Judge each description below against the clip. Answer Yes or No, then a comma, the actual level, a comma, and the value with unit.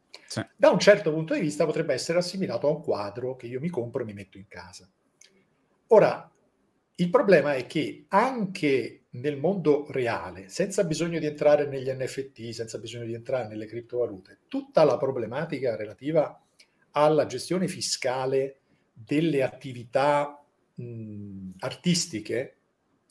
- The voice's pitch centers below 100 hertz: No, medium, 140 Hz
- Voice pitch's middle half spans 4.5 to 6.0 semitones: Yes, wide, 5.5 semitones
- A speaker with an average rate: Yes, average, 140 wpm